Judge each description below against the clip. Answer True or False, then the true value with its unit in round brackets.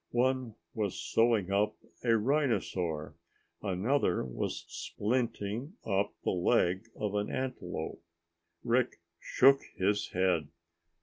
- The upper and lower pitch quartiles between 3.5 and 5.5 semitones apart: True (5.0 semitones)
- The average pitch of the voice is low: True (105 Hz)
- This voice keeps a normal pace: False (105 wpm)